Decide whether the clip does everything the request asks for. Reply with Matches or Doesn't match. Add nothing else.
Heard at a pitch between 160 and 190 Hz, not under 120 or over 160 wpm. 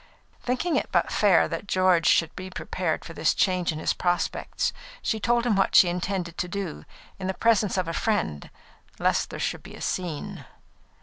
Doesn't match